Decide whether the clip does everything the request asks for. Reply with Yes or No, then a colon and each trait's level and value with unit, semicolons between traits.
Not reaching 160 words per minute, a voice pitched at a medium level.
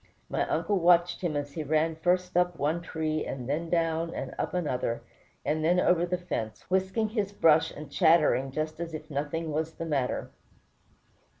No: average, 180 wpm; medium, 165 Hz